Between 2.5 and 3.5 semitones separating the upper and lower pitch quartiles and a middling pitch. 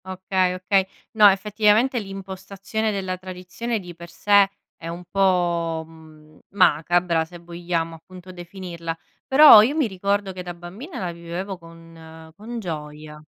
Yes: average, 2.8 semitones; medium, 180 Hz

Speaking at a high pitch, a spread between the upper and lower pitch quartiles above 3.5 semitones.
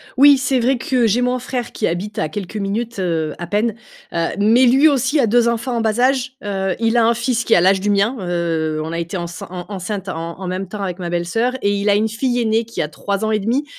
Yes: high, 210 Hz; average, 4.9 semitones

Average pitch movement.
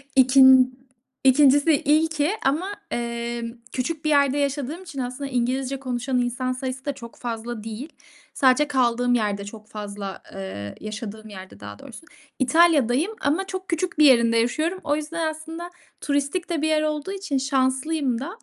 Yes: average, 4.4 semitones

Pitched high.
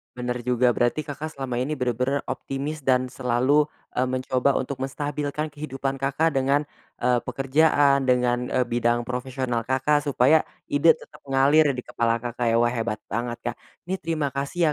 No: low, 130 Hz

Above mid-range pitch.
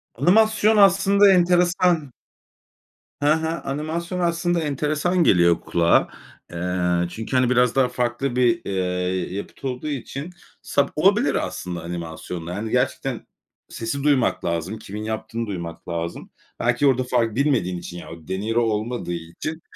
No: low, 120 Hz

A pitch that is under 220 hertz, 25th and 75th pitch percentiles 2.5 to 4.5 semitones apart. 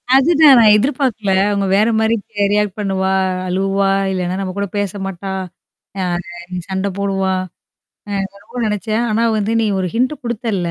Yes: high, 200 Hz; average, 2.8 semitones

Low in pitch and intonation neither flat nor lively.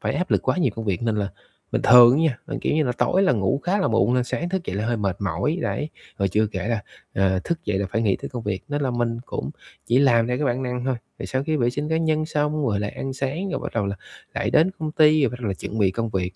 No: low, 125 Hz; wide, 6.2 semitones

